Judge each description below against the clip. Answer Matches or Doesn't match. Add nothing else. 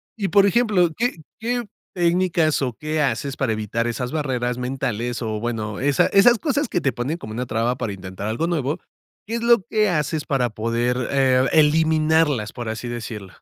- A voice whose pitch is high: Doesn't match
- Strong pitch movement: Matches